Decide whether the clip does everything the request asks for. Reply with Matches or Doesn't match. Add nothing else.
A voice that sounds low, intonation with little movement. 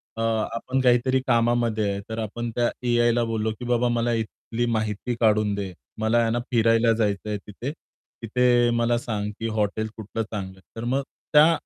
Matches